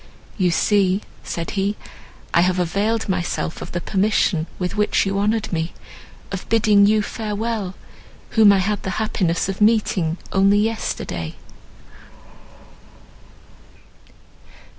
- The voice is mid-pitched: No, high, 200 Hz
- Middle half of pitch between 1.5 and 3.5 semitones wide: Yes, average, 2.8 semitones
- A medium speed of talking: No, slow, 115 wpm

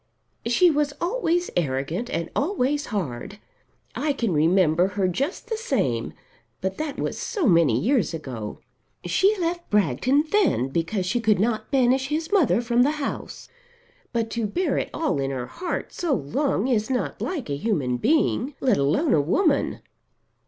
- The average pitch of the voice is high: Yes, high, 235 Hz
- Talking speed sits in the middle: Yes, average, 160 wpm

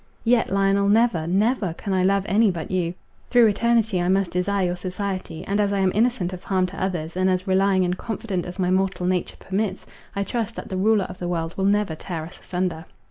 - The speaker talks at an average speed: No, fast, 225 wpm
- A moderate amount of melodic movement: No, narrow, 2.0 semitones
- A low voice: No, high, 190 Hz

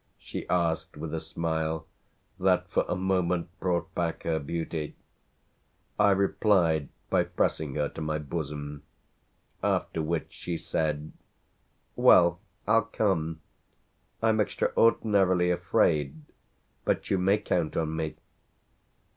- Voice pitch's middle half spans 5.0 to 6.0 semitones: No, average, 2.9 semitones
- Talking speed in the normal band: No, slow, 115 wpm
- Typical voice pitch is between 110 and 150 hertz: No, very low, 85 Hz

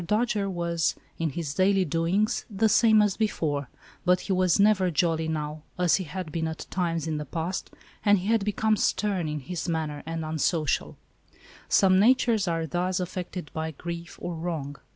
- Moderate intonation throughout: Yes, average, 3.4 semitones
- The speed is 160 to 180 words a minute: Yes, average, 175 wpm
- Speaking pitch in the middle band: Yes, medium, 175 Hz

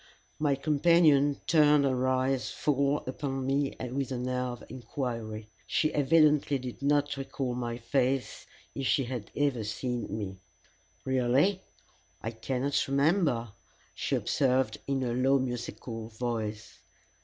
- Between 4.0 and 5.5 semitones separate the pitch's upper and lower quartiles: No, narrow, 2.5 semitones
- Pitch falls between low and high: No, low, 130 Hz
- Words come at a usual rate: No, slow, 130 wpm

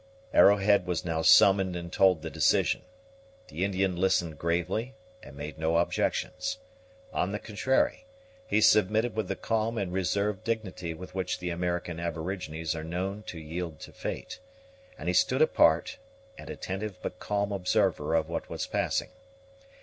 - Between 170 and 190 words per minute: No, average, 155 wpm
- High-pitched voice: No, very low, 90 Hz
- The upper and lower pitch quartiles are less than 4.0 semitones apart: Yes, average, 3.3 semitones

